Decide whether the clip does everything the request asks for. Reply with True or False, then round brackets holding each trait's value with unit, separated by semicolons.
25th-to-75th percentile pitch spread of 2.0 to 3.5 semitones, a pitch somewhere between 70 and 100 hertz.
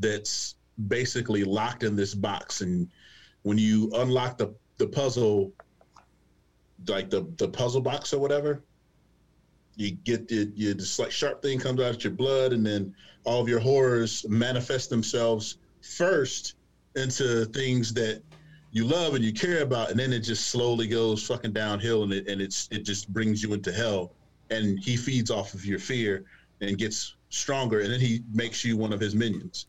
False (3.2 semitones; 110 Hz)